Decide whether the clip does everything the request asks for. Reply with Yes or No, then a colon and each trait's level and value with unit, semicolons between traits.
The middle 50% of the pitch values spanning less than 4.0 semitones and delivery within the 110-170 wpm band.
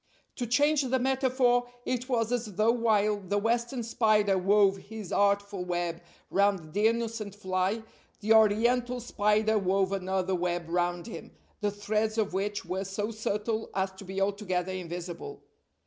Yes: average, 3.1 semitones; average, 150 wpm